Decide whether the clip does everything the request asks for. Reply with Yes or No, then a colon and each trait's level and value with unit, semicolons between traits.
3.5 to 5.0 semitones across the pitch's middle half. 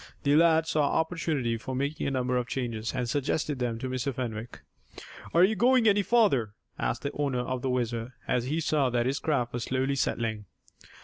Yes: average, 4.1 semitones